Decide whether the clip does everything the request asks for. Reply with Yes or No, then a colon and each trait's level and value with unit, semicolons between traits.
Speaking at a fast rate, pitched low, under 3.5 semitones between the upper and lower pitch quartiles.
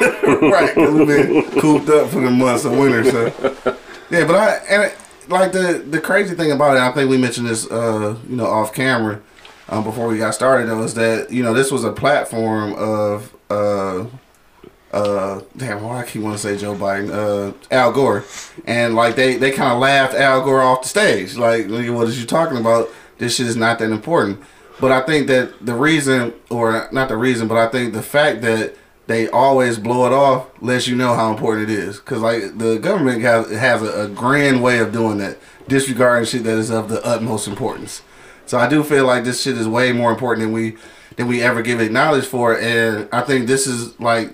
Yes: fast, 220 wpm; low, 120 Hz; average, 2.7 semitones